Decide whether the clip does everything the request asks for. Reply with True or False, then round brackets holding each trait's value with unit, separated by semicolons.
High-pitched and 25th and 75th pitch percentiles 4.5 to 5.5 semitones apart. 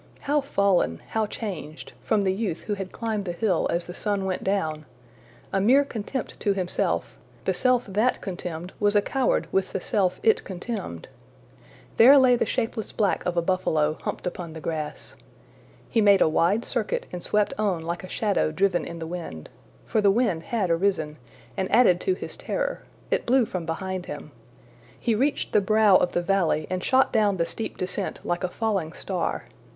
False (195 Hz; 4.0 semitones)